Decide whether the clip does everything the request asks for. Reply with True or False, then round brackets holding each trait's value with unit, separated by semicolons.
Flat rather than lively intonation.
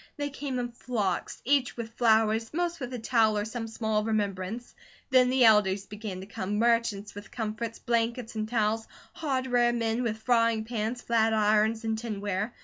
True (2.1 semitones)